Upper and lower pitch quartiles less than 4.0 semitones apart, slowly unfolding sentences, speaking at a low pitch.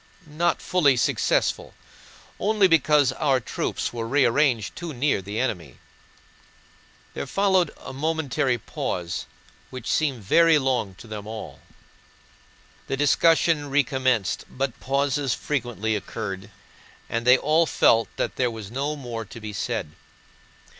No: average, 4.9 semitones; slow, 125 wpm; low, 130 Hz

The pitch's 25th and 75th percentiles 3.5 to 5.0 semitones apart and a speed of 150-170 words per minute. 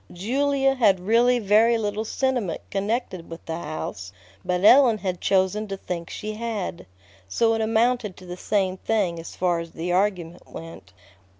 Yes: average, 4.2 semitones; average, 165 wpm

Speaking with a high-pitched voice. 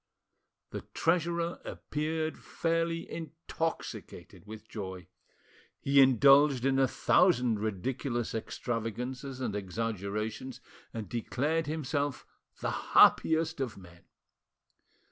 No: low, 130 Hz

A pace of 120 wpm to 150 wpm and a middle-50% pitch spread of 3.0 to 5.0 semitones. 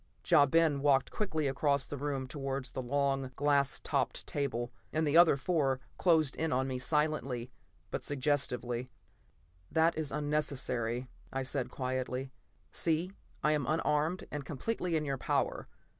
No: average, 145 wpm; narrow, 2.6 semitones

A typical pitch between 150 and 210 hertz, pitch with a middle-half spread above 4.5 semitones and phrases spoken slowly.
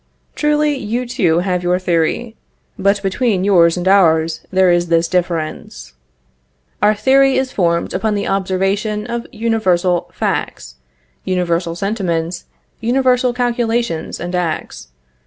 Yes: high, 190 Hz; average, 5.0 semitones; slow, 120 wpm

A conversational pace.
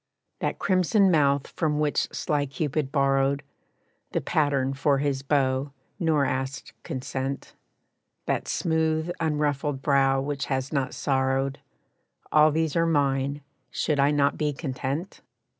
No: slow, 125 wpm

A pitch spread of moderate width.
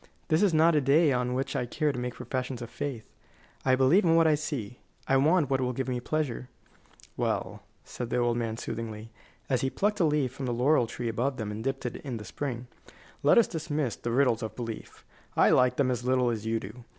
Yes: average, 3.5 semitones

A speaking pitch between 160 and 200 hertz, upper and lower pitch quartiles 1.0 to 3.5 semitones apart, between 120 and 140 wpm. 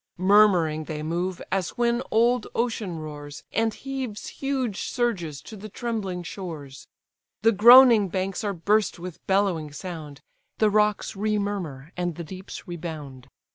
No: high, 190 Hz; average, 5.0 semitones; slow, 135 wpm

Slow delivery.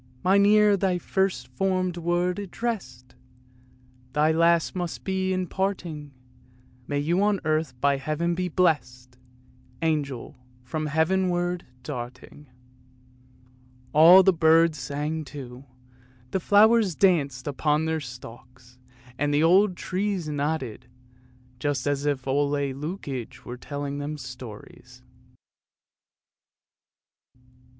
Yes: slow, 110 wpm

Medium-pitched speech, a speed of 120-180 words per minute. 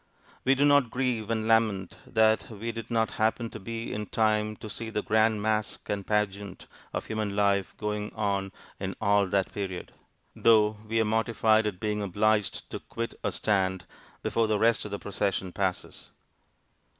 No: low, 105 Hz; average, 175 wpm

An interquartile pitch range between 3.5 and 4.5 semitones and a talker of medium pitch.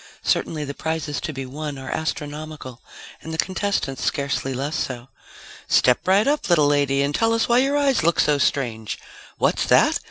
Yes: average, 4.0 semitones; medium, 150 Hz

